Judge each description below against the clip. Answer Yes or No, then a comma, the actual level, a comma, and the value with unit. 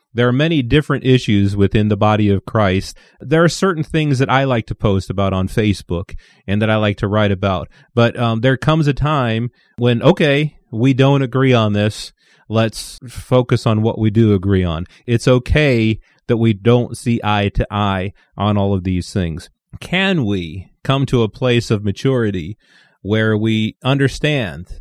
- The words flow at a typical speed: Yes, average, 180 wpm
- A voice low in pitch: Yes, low, 115 Hz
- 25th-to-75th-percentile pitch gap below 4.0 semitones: No, average, 4.5 semitones